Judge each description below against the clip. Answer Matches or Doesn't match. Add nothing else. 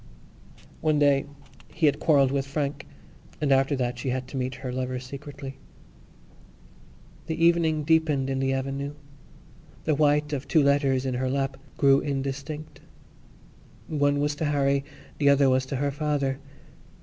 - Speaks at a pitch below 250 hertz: Matches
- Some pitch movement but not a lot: Doesn't match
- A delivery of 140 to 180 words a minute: Matches